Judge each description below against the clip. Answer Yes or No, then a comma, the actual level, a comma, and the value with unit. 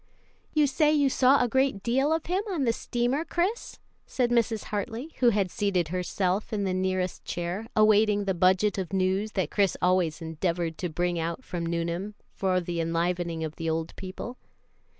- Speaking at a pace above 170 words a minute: Yes, average, 180 wpm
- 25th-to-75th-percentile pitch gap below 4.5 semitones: No, wide, 5.4 semitones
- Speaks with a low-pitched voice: No, high, 195 Hz